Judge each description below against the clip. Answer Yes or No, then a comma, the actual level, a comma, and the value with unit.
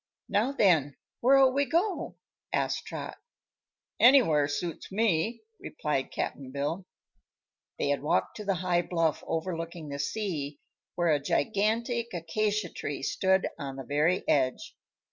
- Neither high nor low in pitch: Yes, medium, 175 Hz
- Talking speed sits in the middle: No, slow, 130 wpm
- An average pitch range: No, wide, 6.7 semitones